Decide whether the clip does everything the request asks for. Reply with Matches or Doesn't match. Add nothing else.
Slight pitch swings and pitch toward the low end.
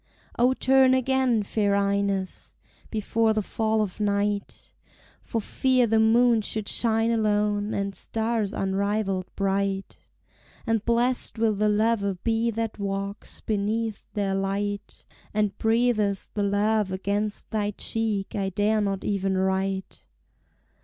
Doesn't match